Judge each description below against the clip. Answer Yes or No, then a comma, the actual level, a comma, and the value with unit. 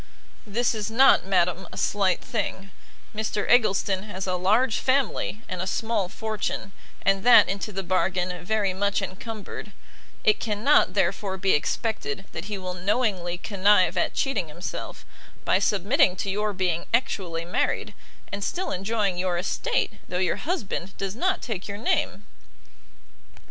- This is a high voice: Yes, high, 200 Hz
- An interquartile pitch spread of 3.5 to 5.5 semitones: No, average, 2.9 semitones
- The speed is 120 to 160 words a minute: Yes, average, 150 wpm